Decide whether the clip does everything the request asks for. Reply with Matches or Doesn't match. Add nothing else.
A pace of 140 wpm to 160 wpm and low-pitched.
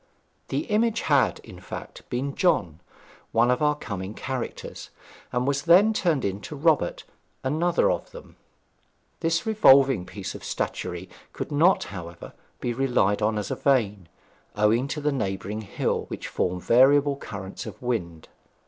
Matches